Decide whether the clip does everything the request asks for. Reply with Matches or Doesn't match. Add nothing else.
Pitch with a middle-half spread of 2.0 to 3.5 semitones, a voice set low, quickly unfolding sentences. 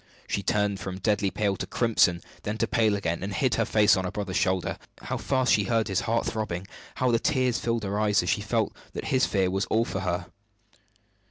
Matches